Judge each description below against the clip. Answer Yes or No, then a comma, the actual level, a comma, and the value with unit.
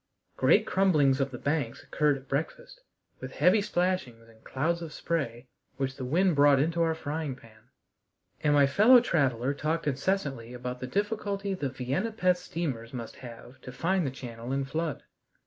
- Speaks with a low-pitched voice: No, medium, 145 Hz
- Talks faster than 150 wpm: Yes, average, 170 wpm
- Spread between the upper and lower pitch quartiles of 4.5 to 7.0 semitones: Yes, average, 5.1 semitones